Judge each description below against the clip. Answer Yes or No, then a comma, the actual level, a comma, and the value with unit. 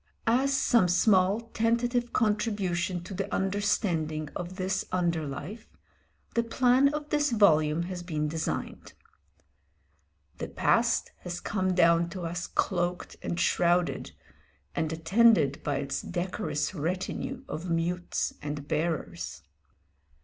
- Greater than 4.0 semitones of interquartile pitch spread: Yes, average, 4.6 semitones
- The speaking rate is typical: No, slow, 120 wpm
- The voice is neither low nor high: Yes, medium, 180 Hz